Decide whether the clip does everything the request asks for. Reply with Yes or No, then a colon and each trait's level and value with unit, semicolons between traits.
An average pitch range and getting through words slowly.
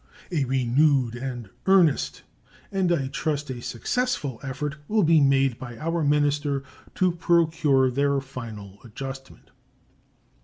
Yes: average, 3.4 semitones; slow, 120 wpm